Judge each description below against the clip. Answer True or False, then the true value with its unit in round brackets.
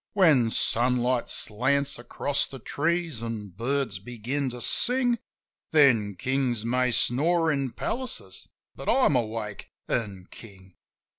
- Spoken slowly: True (125 wpm)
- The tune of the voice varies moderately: True (4.2 semitones)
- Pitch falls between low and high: False (125 Hz)